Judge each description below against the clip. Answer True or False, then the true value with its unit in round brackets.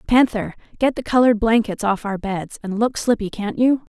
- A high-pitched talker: True (220 Hz)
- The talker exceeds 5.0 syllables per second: True (5.2 syllables/s)